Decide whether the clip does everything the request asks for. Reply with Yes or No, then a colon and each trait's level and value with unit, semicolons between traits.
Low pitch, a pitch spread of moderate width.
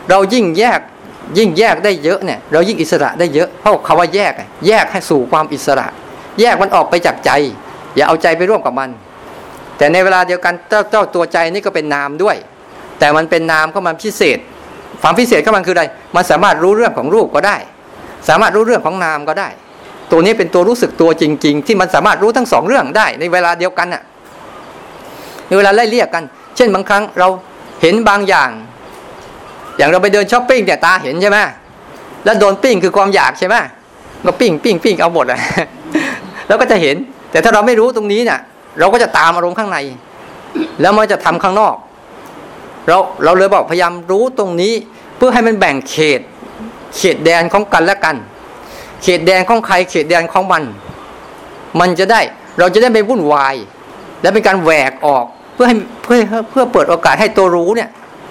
No: high, 190 Hz; average, 4.5 semitones